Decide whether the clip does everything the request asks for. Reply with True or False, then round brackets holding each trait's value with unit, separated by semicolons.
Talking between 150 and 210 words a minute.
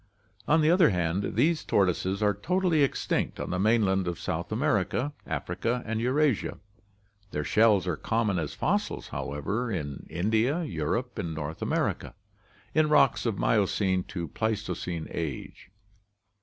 False (140 wpm)